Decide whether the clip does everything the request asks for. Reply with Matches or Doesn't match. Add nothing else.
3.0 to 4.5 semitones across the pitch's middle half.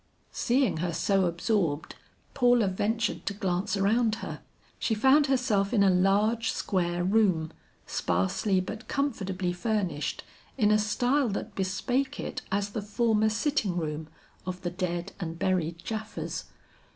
Matches